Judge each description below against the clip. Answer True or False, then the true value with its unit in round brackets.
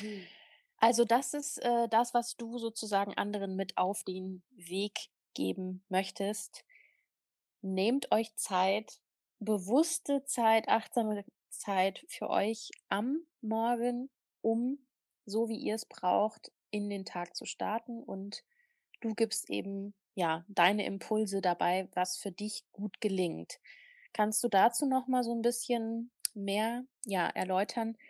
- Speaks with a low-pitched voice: False (220 Hz)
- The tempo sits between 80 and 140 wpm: True (130 wpm)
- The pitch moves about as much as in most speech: True (3.4 semitones)